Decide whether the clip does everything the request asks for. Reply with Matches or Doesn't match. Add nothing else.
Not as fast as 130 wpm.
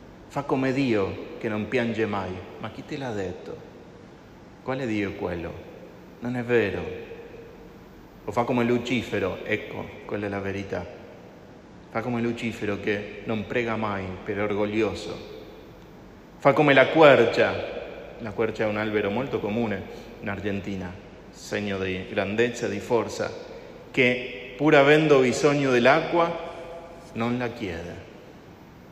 Doesn't match